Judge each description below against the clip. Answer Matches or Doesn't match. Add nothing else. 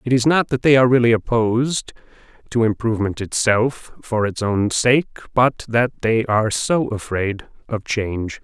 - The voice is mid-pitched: Doesn't match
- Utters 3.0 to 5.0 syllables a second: Matches